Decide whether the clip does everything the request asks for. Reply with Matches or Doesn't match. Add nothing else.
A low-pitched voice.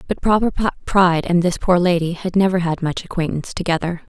Doesn't match